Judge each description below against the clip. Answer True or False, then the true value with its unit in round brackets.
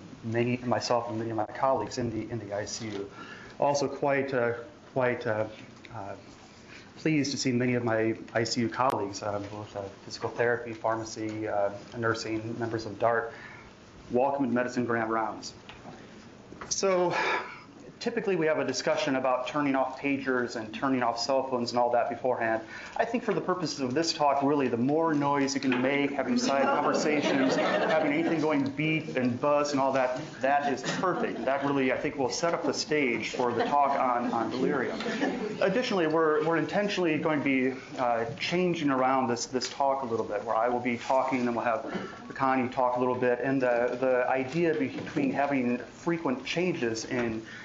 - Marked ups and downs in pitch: False (3.7 semitones)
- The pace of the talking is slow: False (185 wpm)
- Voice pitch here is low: True (125 Hz)